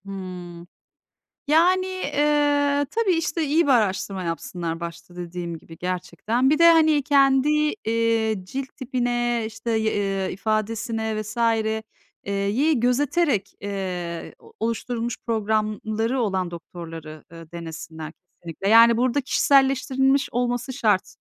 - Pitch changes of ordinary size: No, wide, 6.4 semitones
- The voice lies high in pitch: Yes, high, 225 Hz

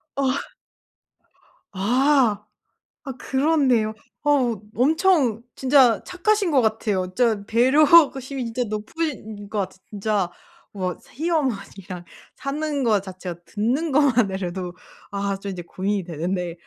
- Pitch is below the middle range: No, high, 225 Hz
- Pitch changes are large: Yes, wide, 6.0 semitones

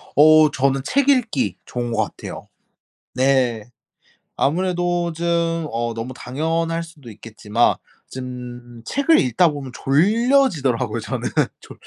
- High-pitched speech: No, medium, 140 Hz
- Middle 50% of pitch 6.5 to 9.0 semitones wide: No, wide, 5.9 semitones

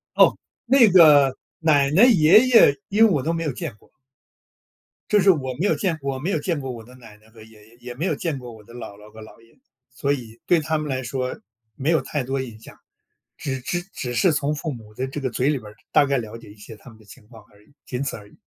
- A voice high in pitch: No, low, 135 Hz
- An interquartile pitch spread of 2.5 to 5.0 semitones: No, wide, 5.4 semitones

